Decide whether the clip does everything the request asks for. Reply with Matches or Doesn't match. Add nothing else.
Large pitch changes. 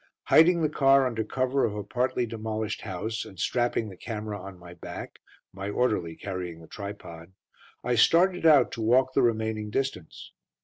Doesn't match